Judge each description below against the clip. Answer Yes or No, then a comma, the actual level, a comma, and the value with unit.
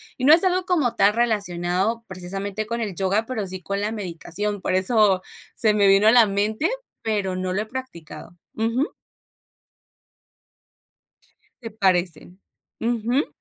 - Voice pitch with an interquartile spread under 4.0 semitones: Yes, average, 3.6 semitones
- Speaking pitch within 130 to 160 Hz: No, high, 210 Hz